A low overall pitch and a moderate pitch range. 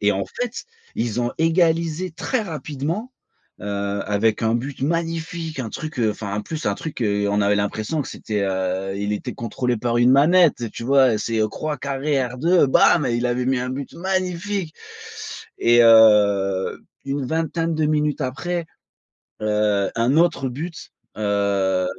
No: low, 130 Hz; wide, 7.3 semitones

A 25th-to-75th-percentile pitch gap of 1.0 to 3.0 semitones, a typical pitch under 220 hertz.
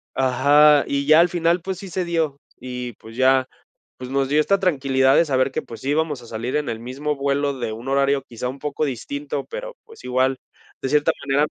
Yes: average, 2.7 semitones; medium, 140 Hz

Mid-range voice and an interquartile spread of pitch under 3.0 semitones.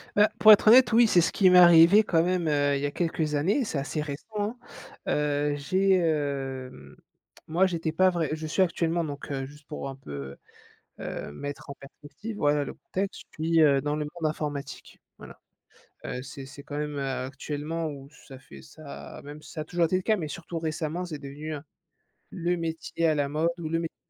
No: medium, 155 Hz; average, 3.3 semitones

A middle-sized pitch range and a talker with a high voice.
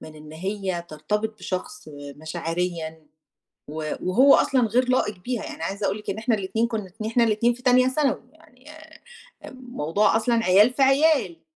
No: wide, 6.5 semitones; high, 210 Hz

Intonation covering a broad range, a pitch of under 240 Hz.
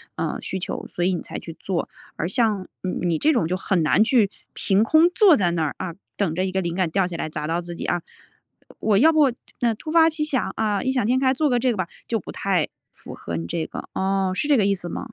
Yes: wide, 6.2 semitones; high, 195 Hz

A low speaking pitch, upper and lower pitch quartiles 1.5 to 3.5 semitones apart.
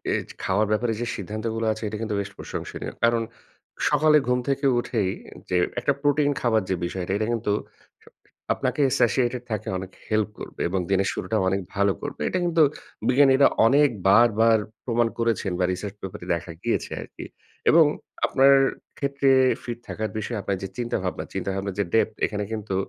No: low, 110 Hz; average, 4.2 semitones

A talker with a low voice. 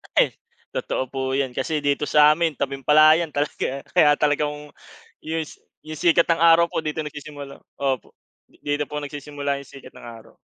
No: medium, 150 Hz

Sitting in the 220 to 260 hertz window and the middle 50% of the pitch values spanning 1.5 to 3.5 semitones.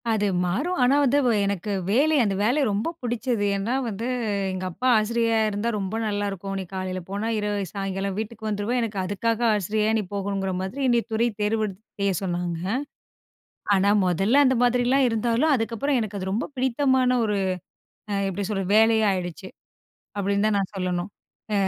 No: high, 210 Hz; average, 3.2 semitones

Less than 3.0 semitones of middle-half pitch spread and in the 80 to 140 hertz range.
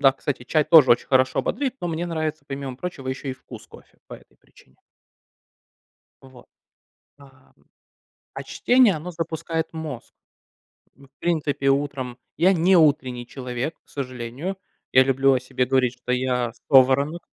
No: average, 3.8 semitones; low, 135 Hz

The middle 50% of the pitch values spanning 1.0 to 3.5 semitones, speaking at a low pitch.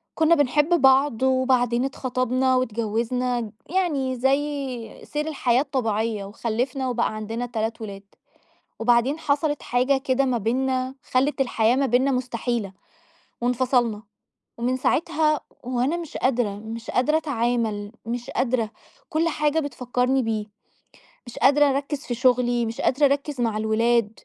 No: average, 2.9 semitones; very high, 250 Hz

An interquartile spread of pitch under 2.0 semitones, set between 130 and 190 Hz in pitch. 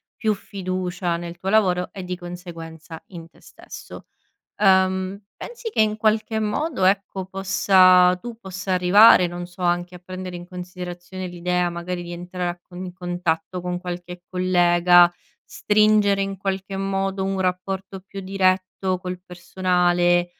Yes: narrow, 1.5 semitones; medium, 185 Hz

